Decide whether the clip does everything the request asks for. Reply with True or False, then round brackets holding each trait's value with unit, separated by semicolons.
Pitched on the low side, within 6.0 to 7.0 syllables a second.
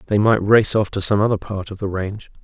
True (100 Hz; 6.1 syllables/s)